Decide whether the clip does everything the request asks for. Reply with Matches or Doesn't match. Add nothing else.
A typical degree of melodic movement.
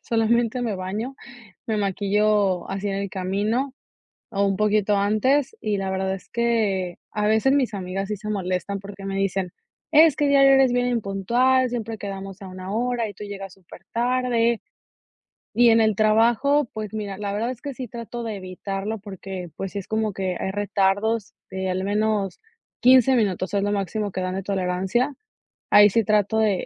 Matches